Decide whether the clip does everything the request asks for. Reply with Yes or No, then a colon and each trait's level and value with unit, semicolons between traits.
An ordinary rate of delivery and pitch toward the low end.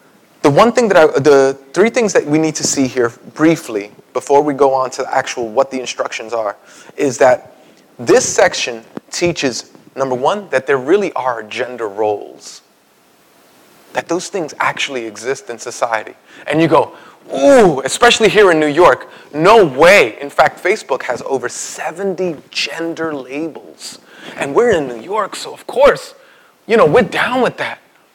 No: average, 165 wpm; medium, 145 Hz